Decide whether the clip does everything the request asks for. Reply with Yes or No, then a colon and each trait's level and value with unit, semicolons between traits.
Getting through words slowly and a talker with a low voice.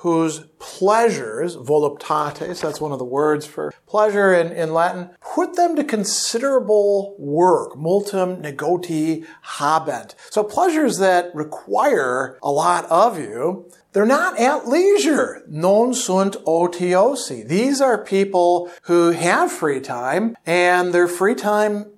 No: slow, 130 wpm; medium, 185 Hz